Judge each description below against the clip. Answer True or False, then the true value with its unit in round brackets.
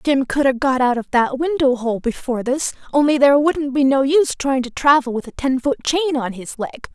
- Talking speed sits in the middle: False (240 wpm)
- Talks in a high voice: True (270 Hz)